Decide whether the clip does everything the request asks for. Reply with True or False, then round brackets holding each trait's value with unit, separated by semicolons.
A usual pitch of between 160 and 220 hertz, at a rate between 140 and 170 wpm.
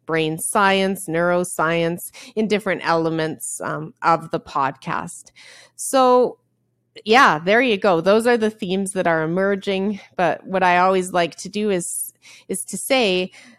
True (190 Hz; 145 wpm)